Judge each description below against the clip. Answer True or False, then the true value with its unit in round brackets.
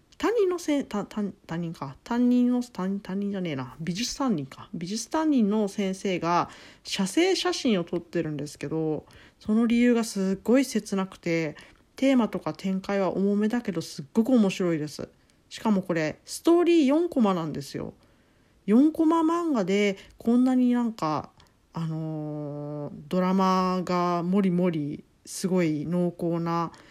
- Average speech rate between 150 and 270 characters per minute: False (290 characters per minute)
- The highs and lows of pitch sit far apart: True (6.0 semitones)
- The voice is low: False (195 Hz)